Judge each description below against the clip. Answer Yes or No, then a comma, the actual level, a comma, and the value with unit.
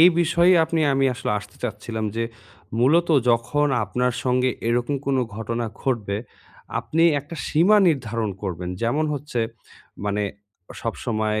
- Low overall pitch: Yes, low, 125 Hz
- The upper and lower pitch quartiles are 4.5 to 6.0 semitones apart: Yes, average, 4.9 semitones